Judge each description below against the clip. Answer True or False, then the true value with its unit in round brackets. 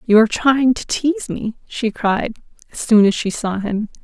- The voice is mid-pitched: False (230 Hz)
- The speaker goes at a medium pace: False (210 wpm)